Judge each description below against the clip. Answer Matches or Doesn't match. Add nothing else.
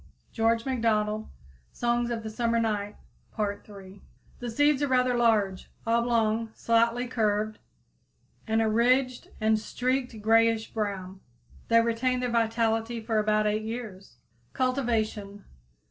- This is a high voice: Matches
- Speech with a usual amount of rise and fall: Doesn't match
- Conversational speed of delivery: Doesn't match